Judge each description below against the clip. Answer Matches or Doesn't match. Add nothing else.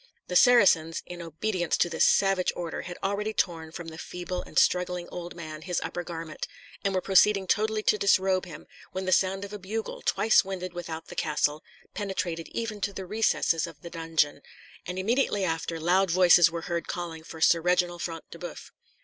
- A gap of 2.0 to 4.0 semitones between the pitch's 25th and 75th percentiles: Matches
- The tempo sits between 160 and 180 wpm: Doesn't match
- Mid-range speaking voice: Matches